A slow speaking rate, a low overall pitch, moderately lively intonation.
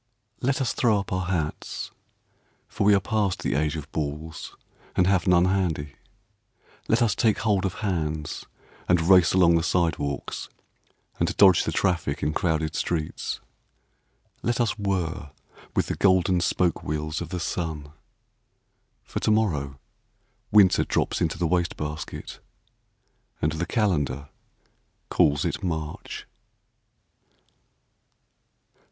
Yes: slow, 130 wpm; very low, 85 Hz; average, 3.9 semitones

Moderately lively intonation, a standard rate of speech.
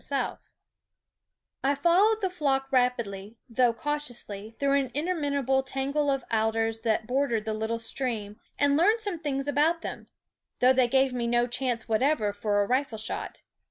Yes: average, 4.1 semitones; average, 180 wpm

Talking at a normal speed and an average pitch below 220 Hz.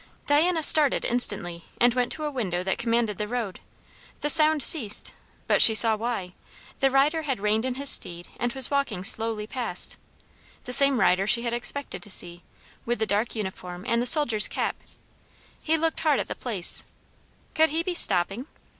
No: average, 180 wpm; high, 240 Hz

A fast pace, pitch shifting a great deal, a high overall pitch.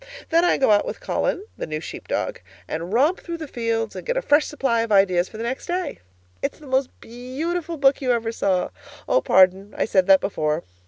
Yes: fast, 220 wpm; wide, 7.3 semitones; high, 235 Hz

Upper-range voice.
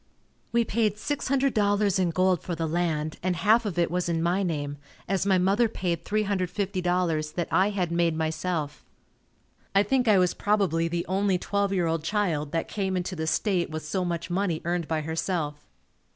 No: medium, 180 Hz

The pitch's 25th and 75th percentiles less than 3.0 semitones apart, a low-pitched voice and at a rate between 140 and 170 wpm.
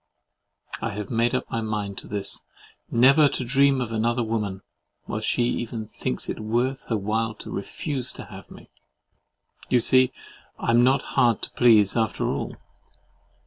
Yes: narrow, 2.5 semitones; low, 115 Hz; average, 165 wpm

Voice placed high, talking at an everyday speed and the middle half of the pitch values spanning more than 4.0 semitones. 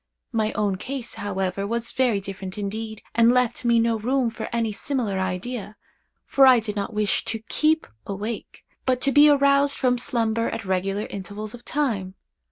No: high, 225 Hz; average, 175 wpm; average, 3.7 semitones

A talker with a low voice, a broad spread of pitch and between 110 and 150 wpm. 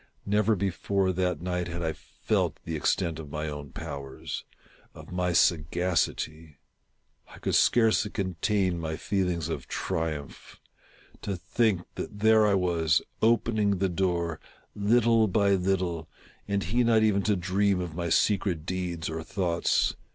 No: very low, 90 Hz; average, 3.5 semitones; average, 145 wpm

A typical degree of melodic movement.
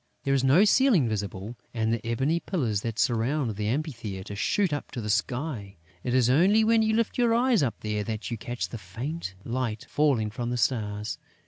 No: wide, 6.1 semitones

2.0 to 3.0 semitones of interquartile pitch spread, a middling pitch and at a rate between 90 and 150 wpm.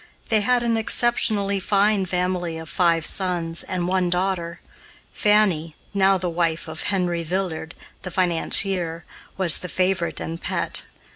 Yes: narrow, 2.5 semitones; medium, 180 Hz; average, 140 wpm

